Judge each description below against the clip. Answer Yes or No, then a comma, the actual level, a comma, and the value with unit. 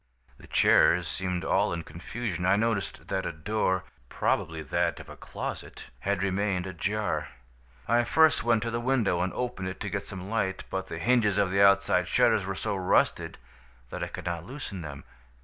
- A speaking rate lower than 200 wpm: Yes, average, 185 wpm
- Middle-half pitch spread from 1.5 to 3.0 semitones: No, average, 3.6 semitones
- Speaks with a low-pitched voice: Yes, very low, 95 Hz